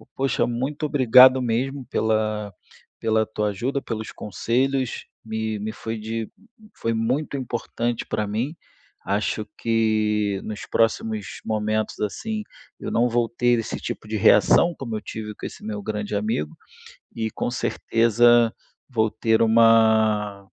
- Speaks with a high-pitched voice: No, low, 110 Hz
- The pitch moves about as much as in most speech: No, narrow, 1.9 semitones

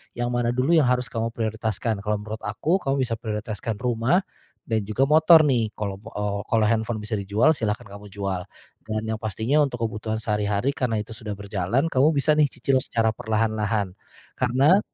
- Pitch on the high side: No, low, 110 Hz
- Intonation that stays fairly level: No, average, 3.1 semitones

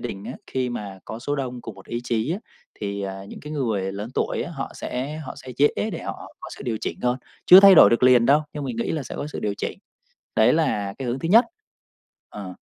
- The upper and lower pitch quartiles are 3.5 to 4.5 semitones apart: No, wide, 5.4 semitones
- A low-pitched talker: Yes, low, 125 Hz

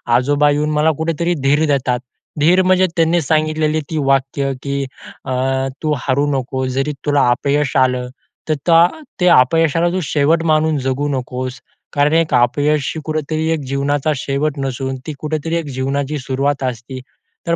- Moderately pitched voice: Yes, medium, 145 Hz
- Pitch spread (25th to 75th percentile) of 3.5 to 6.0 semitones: No, average, 2.8 semitones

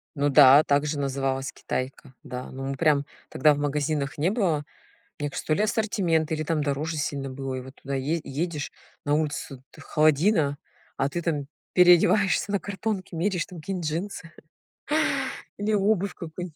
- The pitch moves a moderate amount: Yes, average, 4.0 semitones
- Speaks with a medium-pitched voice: Yes, medium, 155 Hz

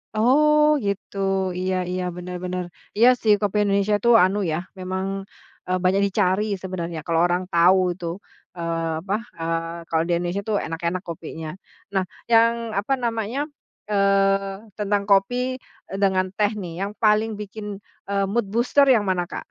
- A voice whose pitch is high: Yes, high, 195 Hz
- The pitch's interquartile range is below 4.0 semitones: Yes, average, 3.0 semitones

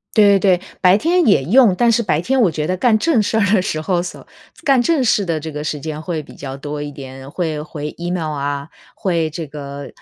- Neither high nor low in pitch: Yes, medium, 170 Hz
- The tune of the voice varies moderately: No, wide, 5.7 semitones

